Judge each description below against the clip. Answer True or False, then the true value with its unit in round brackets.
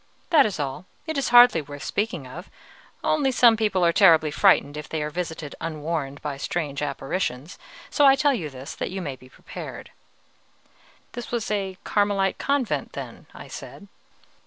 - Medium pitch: True (175 Hz)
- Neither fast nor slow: True (170 wpm)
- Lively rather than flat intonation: True (6.9 semitones)